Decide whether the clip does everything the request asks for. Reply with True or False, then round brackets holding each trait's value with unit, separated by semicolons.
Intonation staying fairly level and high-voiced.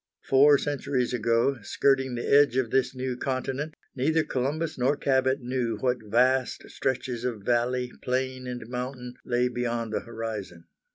False (1.7 semitones; 125 Hz)